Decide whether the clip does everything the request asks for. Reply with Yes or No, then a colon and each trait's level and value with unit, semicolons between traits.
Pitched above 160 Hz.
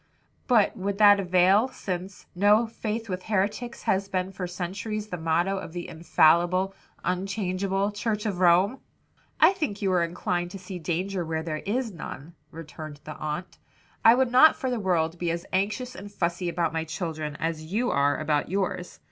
Yes: medium, 185 Hz